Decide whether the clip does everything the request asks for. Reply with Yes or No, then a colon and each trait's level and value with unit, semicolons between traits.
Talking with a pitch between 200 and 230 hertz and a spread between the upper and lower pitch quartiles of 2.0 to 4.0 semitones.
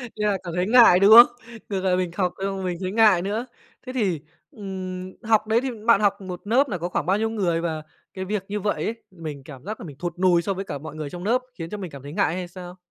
No: high, 190 Hz; average, 3.3 semitones